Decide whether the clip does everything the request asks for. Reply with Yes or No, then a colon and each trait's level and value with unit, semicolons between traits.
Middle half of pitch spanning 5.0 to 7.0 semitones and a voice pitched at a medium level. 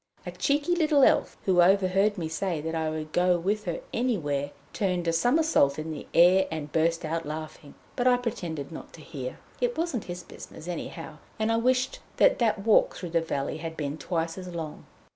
Yes: wide, 5.4 semitones; medium, 175 Hz